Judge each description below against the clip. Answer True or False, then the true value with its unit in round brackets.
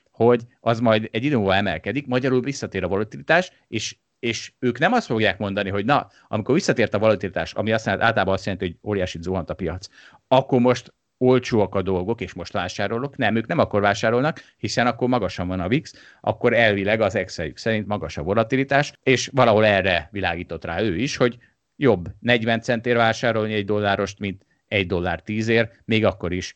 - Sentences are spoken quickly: True (185 wpm)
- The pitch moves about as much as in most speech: True (4.0 semitones)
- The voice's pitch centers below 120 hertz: True (110 Hz)